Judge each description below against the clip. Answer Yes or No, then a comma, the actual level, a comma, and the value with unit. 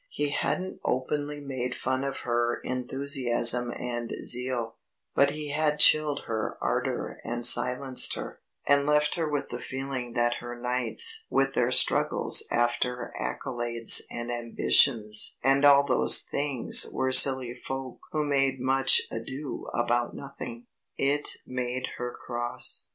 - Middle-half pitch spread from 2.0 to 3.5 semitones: Yes, average, 2.7 semitones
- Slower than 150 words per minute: Yes, slow, 135 wpm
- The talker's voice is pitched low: Yes, low, 130 Hz